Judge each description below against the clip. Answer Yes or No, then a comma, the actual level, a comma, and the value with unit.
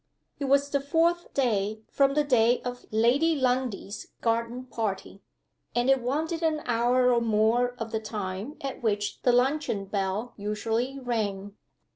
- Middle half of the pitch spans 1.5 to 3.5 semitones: No, average, 3.9 semitones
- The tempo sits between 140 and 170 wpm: Yes, average, 150 wpm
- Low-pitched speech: No, high, 245 Hz